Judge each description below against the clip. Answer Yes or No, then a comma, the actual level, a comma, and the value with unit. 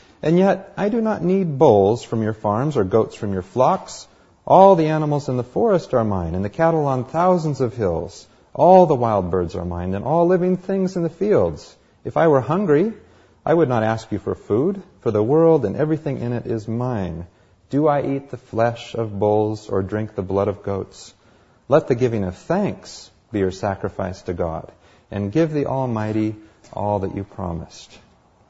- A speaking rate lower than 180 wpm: No, average, 200 wpm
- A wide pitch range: Yes, wide, 7.4 semitones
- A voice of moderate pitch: No, low, 115 Hz